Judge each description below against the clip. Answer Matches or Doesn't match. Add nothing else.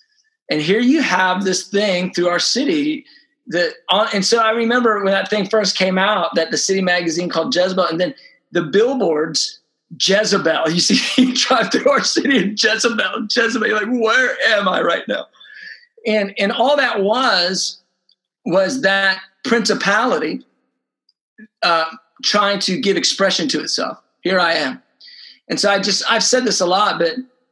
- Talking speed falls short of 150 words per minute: Doesn't match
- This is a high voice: Matches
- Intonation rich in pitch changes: Doesn't match